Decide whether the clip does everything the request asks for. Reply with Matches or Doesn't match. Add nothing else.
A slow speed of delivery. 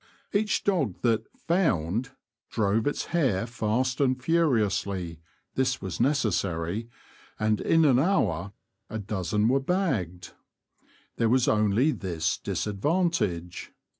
Matches